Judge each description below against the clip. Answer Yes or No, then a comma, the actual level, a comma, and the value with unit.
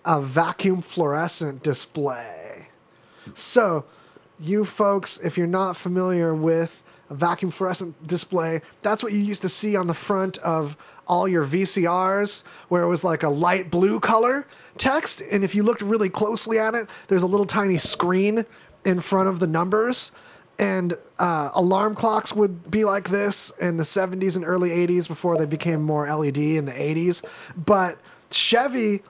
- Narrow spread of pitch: No, average, 3.3 semitones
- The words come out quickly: No, average, 165 wpm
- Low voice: No, medium, 185 Hz